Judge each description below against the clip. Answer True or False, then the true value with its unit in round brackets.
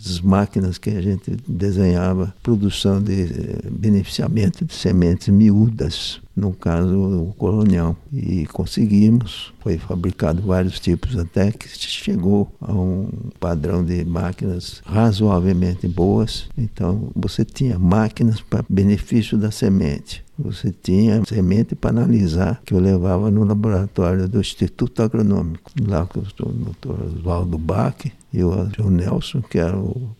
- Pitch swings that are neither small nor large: True (3.1 semitones)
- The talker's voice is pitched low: True (100 Hz)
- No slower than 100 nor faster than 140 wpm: True (130 wpm)